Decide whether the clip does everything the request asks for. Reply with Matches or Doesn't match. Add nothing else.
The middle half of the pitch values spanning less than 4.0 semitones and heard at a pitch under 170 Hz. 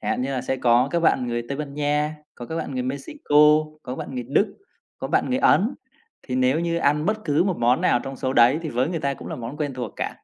Matches